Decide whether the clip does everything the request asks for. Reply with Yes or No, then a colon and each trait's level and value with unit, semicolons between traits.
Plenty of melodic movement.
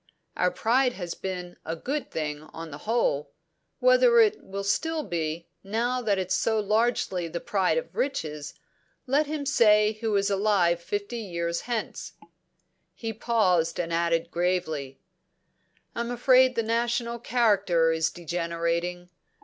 Yes: wide, 5.8 semitones